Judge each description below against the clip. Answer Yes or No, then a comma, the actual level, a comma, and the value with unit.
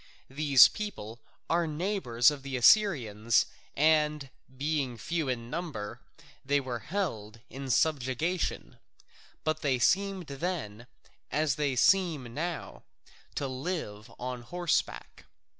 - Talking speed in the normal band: No, slow, 110 wpm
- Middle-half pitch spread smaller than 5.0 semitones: No, wide, 5.4 semitones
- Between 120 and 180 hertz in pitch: Yes, medium, 140 Hz